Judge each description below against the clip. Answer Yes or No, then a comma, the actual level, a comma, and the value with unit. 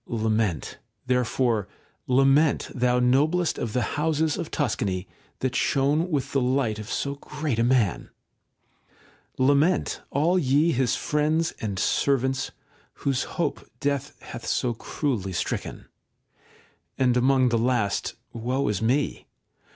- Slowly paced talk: Yes, slow, 125 wpm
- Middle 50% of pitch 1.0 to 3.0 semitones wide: No, average, 3.5 semitones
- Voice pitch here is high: No, low, 130 Hz